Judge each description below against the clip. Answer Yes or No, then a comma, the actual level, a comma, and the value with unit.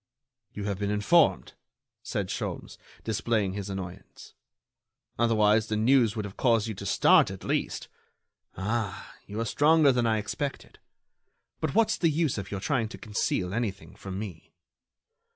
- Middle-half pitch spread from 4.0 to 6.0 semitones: No, average, 3.1 semitones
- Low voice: Yes, low, 110 Hz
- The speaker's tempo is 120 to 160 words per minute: Yes, average, 150 wpm